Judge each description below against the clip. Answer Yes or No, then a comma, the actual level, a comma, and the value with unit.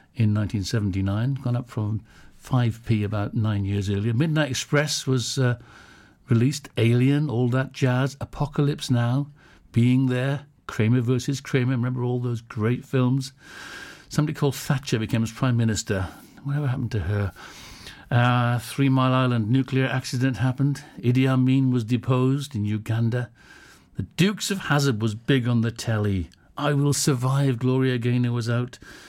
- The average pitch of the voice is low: Yes, low, 125 Hz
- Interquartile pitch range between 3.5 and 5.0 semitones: No, average, 2.9 semitones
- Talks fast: No, average, 145 wpm